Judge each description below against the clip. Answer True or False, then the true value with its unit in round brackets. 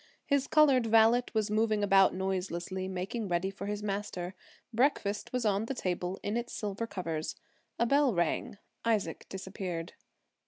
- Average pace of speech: True (150 wpm)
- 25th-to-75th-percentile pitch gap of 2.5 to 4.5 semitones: True (3.4 semitones)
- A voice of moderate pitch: False (205 Hz)